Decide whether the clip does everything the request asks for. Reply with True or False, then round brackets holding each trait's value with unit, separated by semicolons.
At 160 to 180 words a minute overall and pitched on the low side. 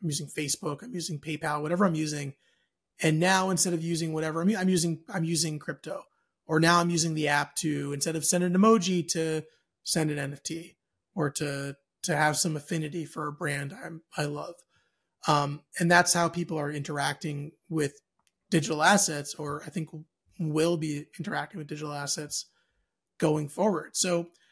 False (170 wpm; 160 Hz)